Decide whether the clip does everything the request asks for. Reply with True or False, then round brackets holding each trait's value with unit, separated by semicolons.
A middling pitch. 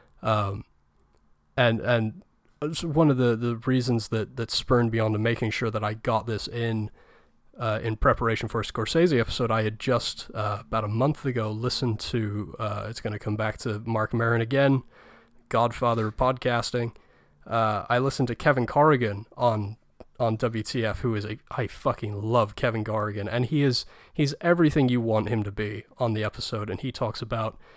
False (115 Hz)